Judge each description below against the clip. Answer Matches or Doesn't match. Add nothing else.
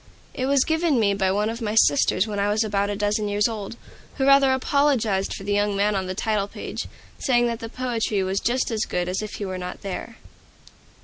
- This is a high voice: Matches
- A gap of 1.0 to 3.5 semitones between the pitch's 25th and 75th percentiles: Matches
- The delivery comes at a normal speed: Doesn't match